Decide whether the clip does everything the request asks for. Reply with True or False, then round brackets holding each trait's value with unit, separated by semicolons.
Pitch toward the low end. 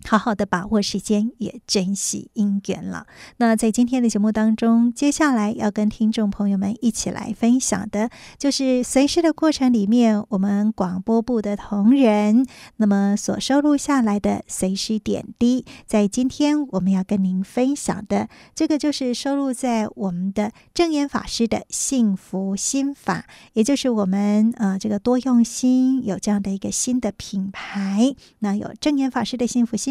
False (225 Hz)